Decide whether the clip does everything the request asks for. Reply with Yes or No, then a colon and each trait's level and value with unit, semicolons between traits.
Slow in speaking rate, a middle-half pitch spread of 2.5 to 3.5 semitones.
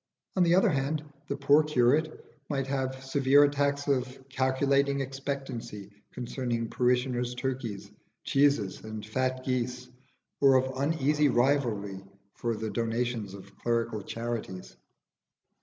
Yes: slow, 120 wpm; average, 2.9 semitones